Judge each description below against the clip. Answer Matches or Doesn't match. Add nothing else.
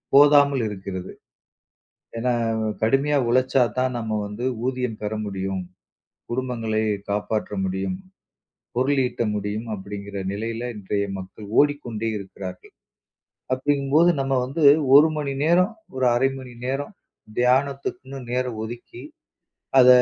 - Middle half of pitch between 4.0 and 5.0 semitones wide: Matches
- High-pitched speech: Doesn't match